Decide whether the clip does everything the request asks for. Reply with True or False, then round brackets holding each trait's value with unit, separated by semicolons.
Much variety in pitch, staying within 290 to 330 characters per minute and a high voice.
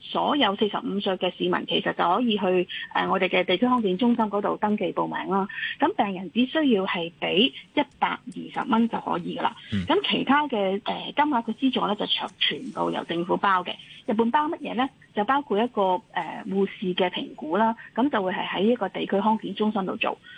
False (4.5 semitones; 310 characters per minute; 215 Hz)